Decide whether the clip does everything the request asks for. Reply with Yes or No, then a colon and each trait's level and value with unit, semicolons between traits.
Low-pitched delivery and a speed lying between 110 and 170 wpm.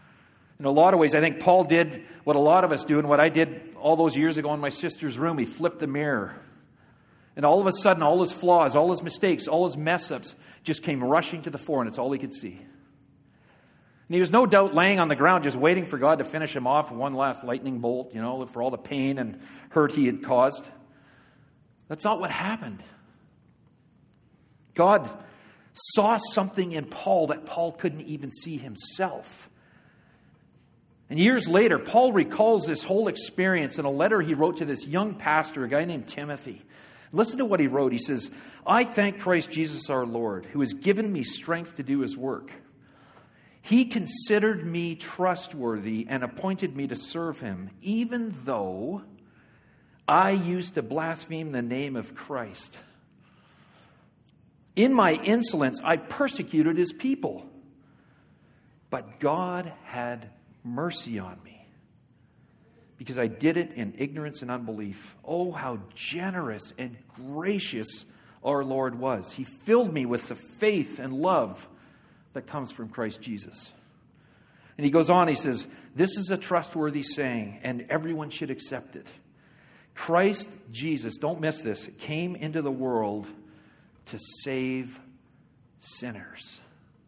No: medium, 155 Hz; average, 165 wpm